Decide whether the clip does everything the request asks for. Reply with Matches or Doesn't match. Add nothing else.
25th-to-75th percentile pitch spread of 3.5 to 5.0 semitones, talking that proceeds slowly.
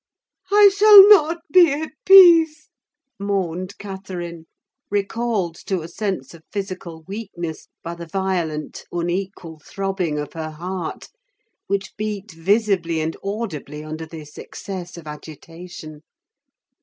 Matches